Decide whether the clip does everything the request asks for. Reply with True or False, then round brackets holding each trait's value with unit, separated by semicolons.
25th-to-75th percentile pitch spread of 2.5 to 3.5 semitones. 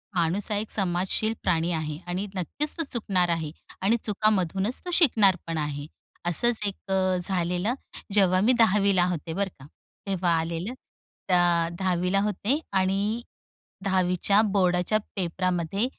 True (3.0 semitones)